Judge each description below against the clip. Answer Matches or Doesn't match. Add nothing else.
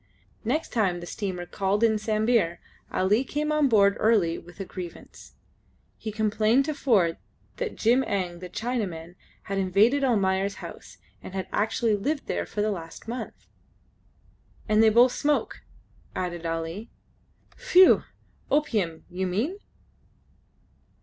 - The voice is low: Doesn't match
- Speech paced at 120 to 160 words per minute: Matches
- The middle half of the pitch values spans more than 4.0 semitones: Matches